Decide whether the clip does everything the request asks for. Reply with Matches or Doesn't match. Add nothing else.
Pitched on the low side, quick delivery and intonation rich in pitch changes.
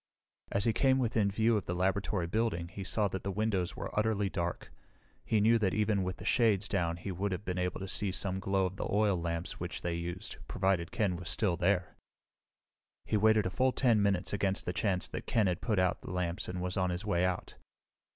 Doesn't match